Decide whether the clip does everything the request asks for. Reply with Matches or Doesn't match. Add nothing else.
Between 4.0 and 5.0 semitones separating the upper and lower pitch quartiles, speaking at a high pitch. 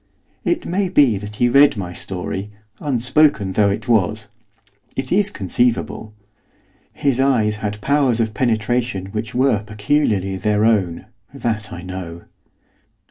Doesn't match